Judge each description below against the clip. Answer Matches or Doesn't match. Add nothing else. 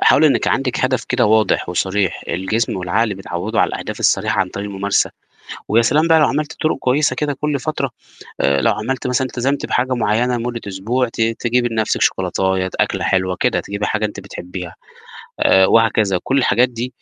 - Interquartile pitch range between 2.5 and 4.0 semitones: Doesn't match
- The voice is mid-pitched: Doesn't match